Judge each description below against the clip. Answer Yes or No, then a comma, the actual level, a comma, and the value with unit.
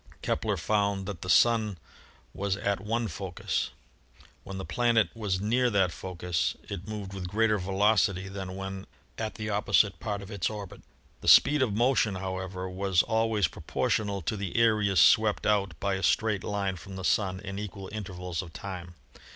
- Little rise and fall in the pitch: Yes, narrow, 2.2 semitones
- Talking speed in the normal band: Yes, average, 180 wpm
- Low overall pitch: Yes, low, 100 Hz